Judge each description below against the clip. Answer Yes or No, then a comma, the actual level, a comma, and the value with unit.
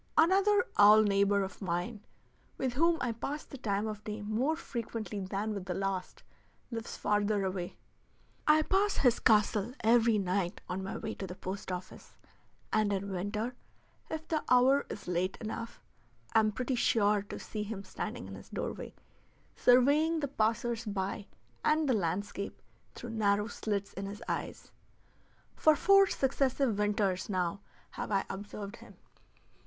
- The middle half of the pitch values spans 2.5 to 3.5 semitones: No, average, 3.9 semitones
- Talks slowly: No, average, 155 wpm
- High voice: Yes, high, 215 Hz